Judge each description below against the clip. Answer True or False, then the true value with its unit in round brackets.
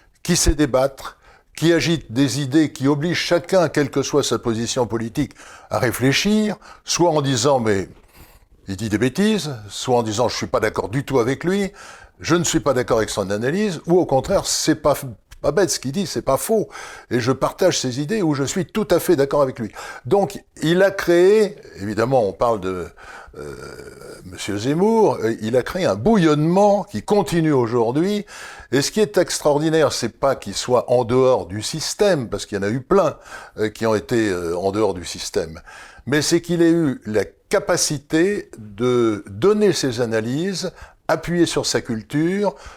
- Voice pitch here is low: False (145 Hz)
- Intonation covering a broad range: True (6.5 semitones)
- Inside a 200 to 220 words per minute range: False (185 wpm)